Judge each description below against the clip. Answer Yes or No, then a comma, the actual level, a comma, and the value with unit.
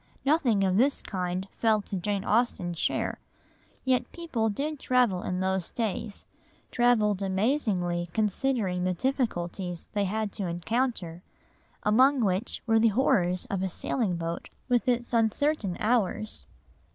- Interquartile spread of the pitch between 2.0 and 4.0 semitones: No, average, 5.0 semitones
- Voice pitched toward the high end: Yes, high, 210 Hz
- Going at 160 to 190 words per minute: No, slow, 135 wpm